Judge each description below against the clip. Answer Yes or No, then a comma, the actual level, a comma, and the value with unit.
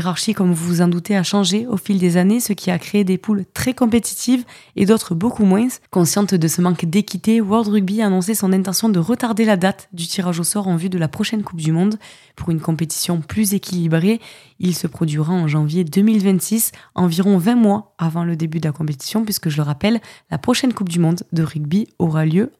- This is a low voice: No, high, 190 Hz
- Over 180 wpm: Yes, fast, 220 wpm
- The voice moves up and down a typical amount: Yes, average, 3.8 semitones